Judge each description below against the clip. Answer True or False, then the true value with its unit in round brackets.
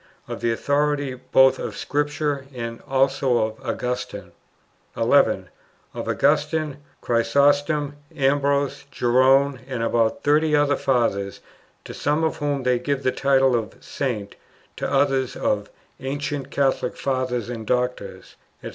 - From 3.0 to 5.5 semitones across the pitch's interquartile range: False (2.6 semitones)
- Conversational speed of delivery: False (130 wpm)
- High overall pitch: False (135 Hz)